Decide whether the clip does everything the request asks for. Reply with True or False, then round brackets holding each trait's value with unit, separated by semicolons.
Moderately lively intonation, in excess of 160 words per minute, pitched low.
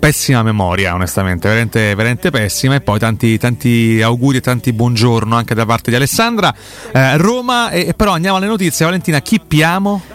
False (7.4 semitones; 170 wpm; 125 Hz)